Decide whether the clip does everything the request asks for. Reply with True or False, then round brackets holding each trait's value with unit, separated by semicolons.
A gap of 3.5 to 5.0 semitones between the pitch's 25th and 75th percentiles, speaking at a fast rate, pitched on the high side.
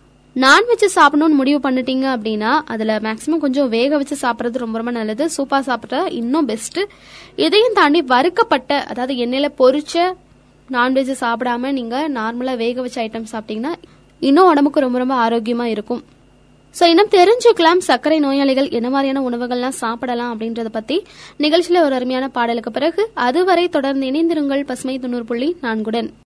True (4.4 semitones; 140 wpm; 265 Hz)